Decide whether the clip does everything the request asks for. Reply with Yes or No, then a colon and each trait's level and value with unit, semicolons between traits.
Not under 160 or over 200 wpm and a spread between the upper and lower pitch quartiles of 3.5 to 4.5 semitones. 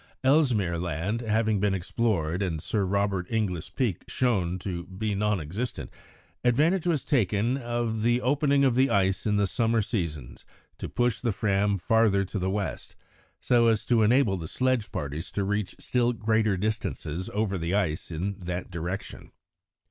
Yes: average, 165 wpm; average, 4.2 semitones